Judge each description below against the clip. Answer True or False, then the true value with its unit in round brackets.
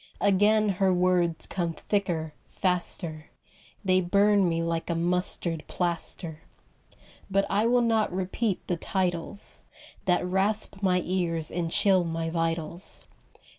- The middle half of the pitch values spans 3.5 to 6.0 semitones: False (2.9 semitones)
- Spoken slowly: True (125 wpm)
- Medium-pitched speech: True (180 Hz)